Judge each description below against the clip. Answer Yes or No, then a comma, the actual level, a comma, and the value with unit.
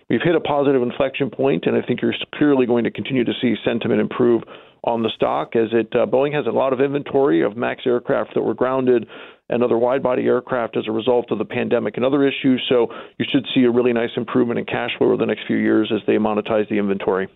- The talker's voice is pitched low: Yes, low, 120 Hz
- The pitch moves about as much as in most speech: Yes, average, 3.7 semitones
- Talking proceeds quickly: Yes, fast, 245 wpm